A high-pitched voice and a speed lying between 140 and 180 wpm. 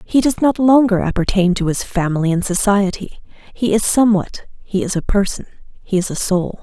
No: high, 200 Hz; average, 190 wpm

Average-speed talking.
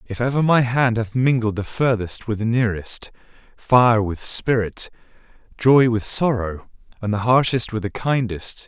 Yes: average, 160 wpm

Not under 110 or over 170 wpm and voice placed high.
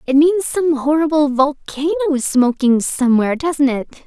Yes: slow, 135 wpm; very high, 285 Hz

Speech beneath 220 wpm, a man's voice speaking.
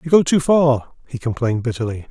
Yes: average, 200 wpm; male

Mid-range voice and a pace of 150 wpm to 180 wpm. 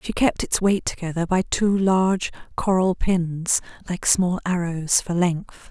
Yes: medium, 180 Hz; average, 160 wpm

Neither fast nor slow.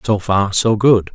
No: fast, 210 wpm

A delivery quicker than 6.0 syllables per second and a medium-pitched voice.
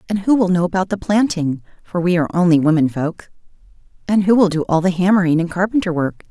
Yes: 6.4 syllables/s; medium, 180 Hz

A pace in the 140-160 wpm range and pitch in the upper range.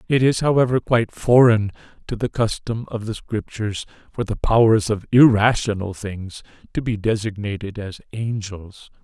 No: average, 145 wpm; low, 110 Hz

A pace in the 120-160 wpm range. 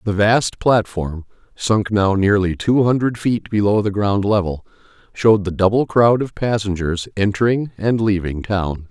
Yes: average, 155 wpm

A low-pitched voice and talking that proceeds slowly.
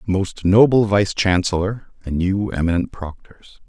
Yes: very low, 95 Hz; slow, 130 wpm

